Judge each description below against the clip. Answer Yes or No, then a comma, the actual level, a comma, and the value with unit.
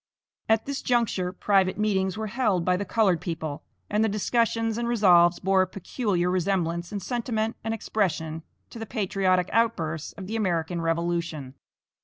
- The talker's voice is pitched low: No, high, 190 Hz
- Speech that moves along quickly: No, average, 160 wpm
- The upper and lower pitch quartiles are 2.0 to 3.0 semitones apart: No, average, 4.2 semitones